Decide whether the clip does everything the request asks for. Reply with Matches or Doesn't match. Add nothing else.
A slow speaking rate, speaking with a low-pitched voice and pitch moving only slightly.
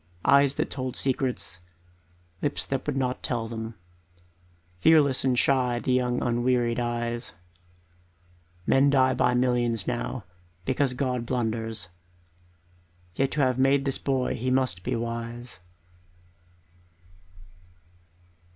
Matches